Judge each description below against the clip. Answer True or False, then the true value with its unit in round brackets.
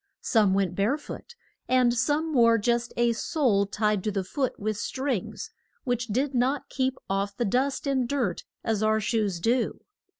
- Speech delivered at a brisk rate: False (170 wpm)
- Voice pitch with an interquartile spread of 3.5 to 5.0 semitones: True (3.9 semitones)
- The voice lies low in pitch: False (235 Hz)